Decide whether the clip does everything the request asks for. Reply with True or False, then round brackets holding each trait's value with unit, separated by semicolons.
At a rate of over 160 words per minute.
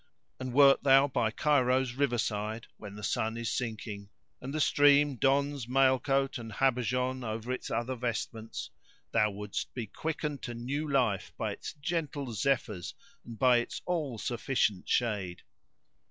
False (155 wpm)